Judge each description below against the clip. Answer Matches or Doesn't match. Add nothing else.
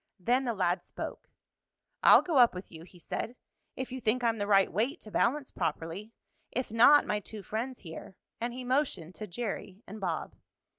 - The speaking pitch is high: Matches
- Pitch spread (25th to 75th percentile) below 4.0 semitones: Doesn't match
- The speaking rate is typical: Matches